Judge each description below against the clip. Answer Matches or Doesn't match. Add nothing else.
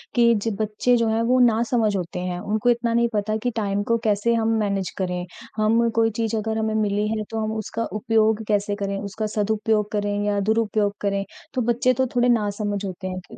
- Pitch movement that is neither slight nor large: Doesn't match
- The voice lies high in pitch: Matches